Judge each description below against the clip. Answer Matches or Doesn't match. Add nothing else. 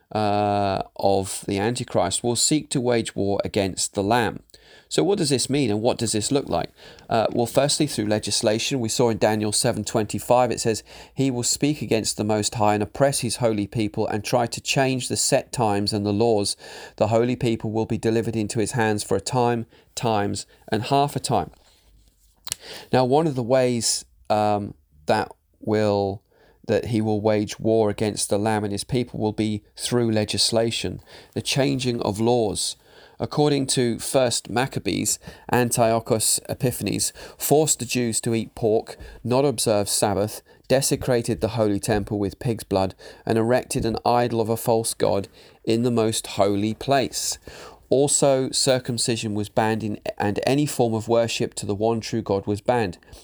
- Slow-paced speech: Doesn't match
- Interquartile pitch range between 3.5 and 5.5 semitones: Doesn't match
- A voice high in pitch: Doesn't match